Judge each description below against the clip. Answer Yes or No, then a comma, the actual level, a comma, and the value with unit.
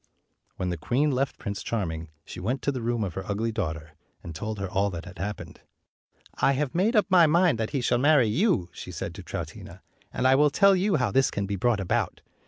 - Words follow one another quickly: Yes, fast, 230 wpm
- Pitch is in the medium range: No, low, 115 Hz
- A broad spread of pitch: Yes, wide, 6.8 semitones